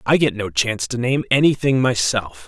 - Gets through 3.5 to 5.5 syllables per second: Yes, 5.2 syllables/s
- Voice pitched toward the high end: No, low, 120 Hz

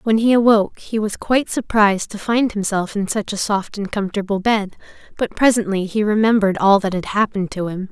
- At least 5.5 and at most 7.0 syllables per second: Yes, 5.9 syllables/s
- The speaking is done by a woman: Yes, female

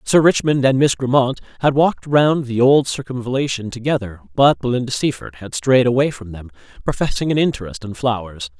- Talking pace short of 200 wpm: Yes, average, 175 wpm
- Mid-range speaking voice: No, low, 125 Hz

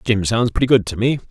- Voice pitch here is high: No, low, 115 Hz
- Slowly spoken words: No, fast, 275 wpm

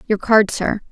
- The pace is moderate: Yes, average, 195 wpm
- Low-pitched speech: No, high, 210 Hz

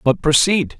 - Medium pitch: Yes, medium, 155 Hz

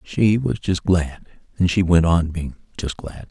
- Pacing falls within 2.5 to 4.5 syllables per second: Yes, 4.1 syllables/s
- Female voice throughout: No, male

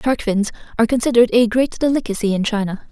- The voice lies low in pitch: No, high, 225 Hz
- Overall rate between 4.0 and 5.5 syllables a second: No, 6.6 syllables/s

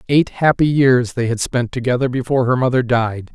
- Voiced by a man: Yes, male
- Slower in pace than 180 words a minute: No, average, 200 wpm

